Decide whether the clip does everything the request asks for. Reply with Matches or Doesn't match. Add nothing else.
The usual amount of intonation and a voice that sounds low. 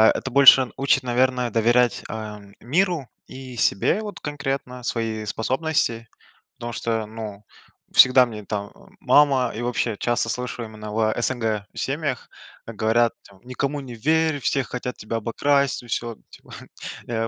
Matches